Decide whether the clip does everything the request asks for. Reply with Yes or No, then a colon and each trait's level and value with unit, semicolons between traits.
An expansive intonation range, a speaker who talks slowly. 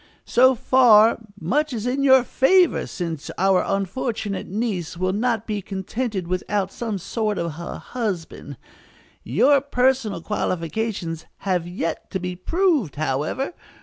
Yes: wide, 5.7 semitones; slow, 130 wpm